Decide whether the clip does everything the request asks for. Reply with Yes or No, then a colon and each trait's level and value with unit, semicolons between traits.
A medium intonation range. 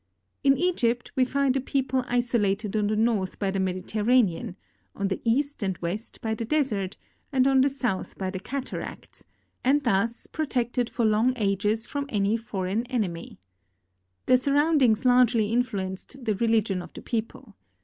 Yes: average, 4.3 semitones